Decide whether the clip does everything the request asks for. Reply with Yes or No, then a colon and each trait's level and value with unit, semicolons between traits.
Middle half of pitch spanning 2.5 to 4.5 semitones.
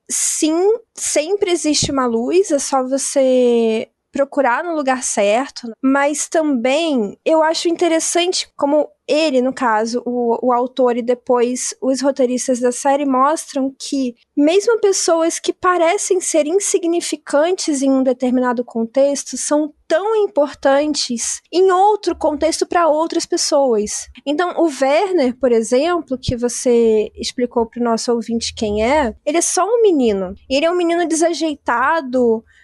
No: average, 5.0 semitones